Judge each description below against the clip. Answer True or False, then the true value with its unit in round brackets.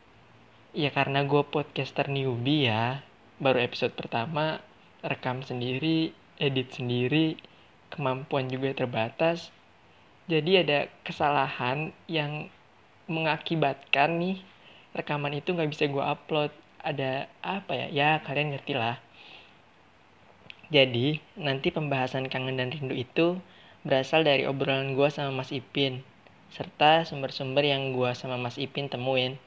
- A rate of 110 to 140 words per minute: True (115 wpm)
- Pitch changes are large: False (2.8 semitones)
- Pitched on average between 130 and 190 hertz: True (140 Hz)